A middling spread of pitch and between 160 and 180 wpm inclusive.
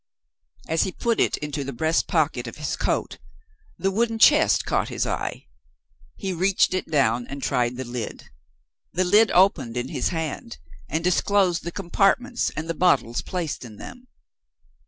No: wide, 6.2 semitones; average, 165 wpm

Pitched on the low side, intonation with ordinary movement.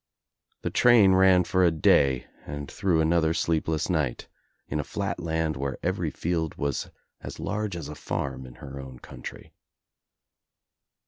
Yes: very low, 80 Hz; average, 4.2 semitones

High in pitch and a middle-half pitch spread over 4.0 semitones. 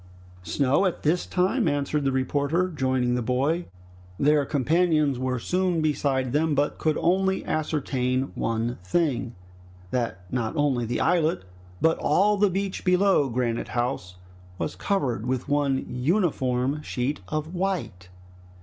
No: medium, 145 Hz; average, 5.1 semitones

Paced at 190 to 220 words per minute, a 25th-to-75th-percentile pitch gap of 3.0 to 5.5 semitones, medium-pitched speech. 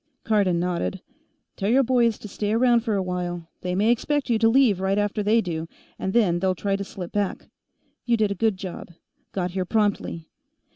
No: average, 200 wpm; average, 3.8 semitones; high, 200 Hz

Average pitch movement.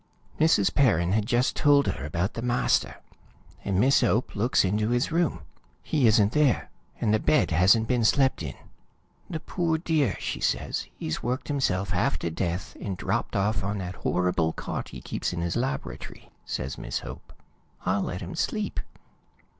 No: wide, 6.3 semitones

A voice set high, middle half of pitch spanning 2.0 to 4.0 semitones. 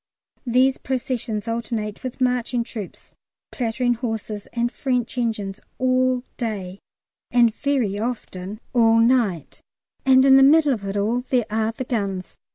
Yes: high, 235 Hz; average, 3.1 semitones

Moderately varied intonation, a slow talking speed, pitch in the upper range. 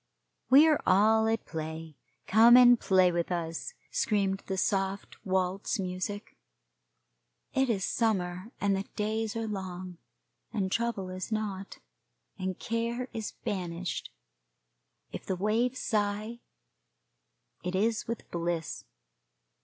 Yes: average, 3.5 semitones; slow, 120 wpm; high, 200 Hz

